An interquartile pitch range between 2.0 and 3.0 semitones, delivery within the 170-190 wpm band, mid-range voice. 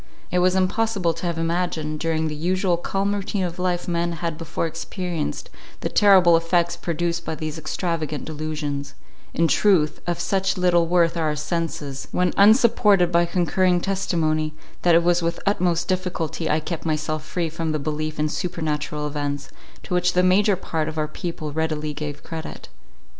Yes: narrow, 2.5 semitones; average, 175 wpm; medium, 170 Hz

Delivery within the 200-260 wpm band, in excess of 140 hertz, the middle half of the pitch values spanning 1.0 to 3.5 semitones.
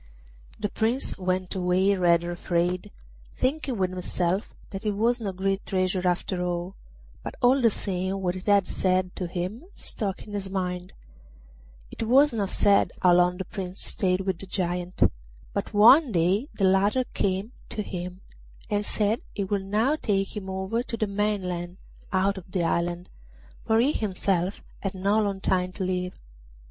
No: average, 170 wpm; high, 190 Hz; narrow, 2.4 semitones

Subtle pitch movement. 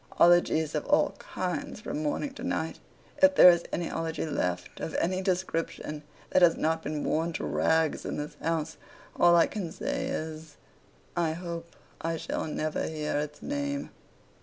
Yes: narrow, 2.0 semitones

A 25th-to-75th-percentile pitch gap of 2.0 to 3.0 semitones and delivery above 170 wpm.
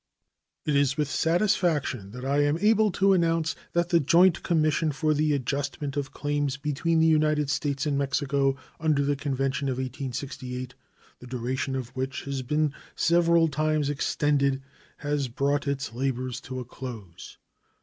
No: narrow, 2.6 semitones; average, 155 wpm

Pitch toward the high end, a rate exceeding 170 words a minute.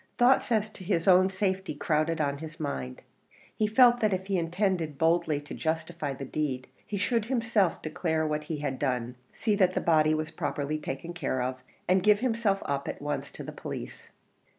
No: medium, 165 Hz; average, 195 wpm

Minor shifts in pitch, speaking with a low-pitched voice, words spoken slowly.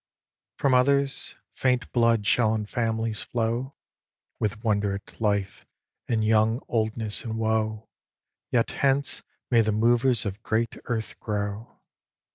Yes: narrow, 2.0 semitones; low, 110 Hz; slow, 125 wpm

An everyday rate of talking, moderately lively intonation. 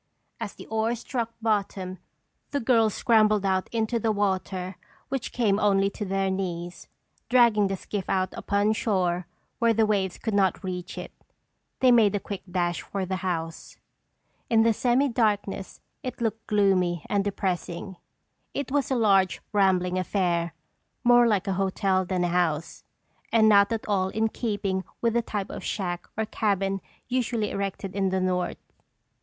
Yes: average, 160 wpm; average, 3.0 semitones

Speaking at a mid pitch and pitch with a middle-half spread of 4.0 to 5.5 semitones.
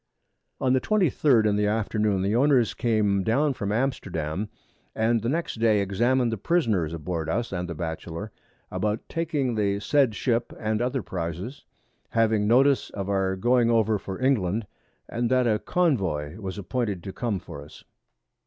No: low, 110 Hz; average, 4.3 semitones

